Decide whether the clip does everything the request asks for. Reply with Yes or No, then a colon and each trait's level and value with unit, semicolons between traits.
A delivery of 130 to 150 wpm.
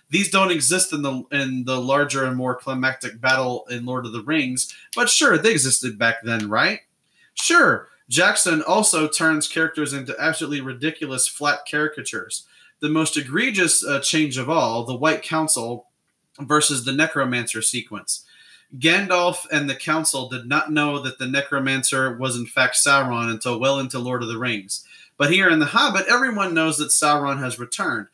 No: average, 170 wpm